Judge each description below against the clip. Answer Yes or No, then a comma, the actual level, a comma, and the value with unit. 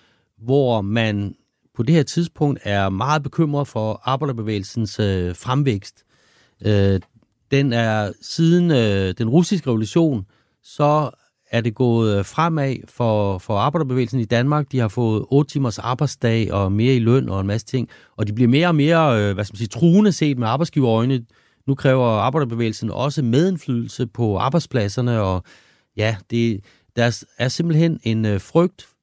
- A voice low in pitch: Yes, low, 120 Hz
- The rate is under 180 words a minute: Yes, slow, 145 wpm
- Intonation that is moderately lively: Yes, average, 4.9 semitones